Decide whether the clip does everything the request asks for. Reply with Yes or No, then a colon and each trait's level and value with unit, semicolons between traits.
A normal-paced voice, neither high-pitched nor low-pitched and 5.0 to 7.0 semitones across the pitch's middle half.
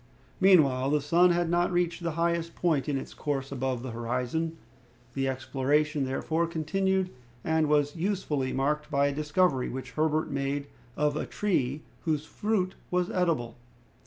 No: average, 155 wpm; medium, 150 Hz; average, 3.9 semitones